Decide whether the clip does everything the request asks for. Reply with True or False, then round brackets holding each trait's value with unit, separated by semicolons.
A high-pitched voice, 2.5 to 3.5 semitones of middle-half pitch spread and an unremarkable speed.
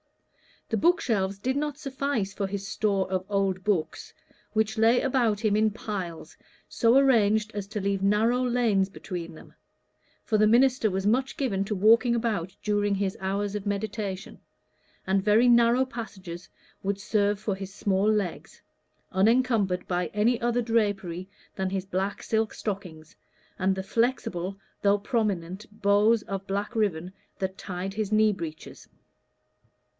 True (205 Hz; 2.9 semitones; 150 wpm)